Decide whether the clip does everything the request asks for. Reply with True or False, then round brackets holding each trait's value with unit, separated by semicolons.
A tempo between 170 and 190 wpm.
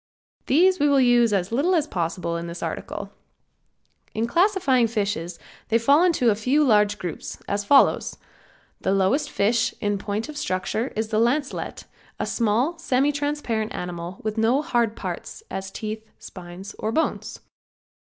False (155 wpm)